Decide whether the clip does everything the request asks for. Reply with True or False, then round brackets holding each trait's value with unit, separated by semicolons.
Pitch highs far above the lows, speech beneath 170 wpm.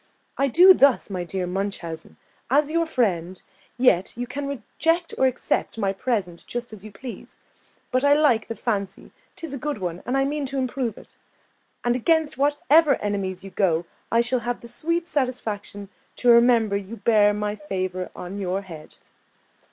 False (5.7 semitones; 175 wpm)